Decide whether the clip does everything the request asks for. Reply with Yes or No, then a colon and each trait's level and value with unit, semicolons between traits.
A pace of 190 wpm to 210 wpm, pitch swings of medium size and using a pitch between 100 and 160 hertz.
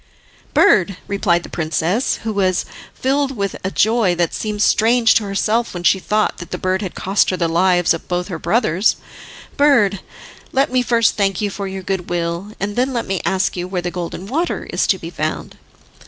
No: average, 200 wpm; average, 3.8 semitones; high, 195 Hz